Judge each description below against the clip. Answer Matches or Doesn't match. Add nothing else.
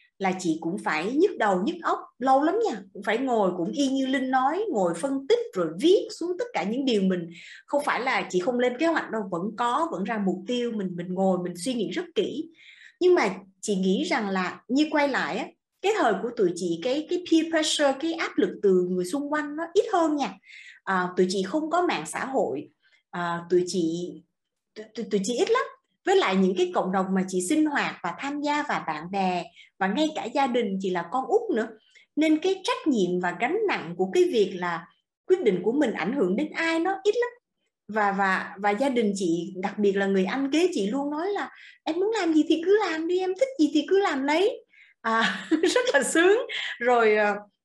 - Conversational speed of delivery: Matches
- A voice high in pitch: Matches